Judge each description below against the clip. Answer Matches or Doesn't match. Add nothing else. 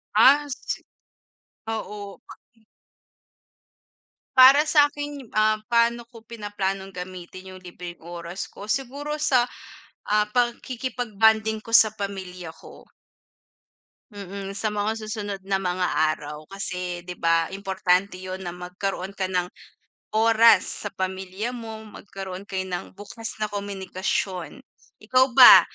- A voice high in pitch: Matches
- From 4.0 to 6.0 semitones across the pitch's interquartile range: Doesn't match